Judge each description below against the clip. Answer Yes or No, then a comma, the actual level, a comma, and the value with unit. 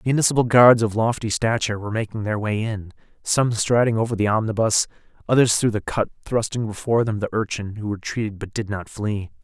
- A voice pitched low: Yes, low, 110 Hz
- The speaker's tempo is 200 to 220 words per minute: No, average, 190 wpm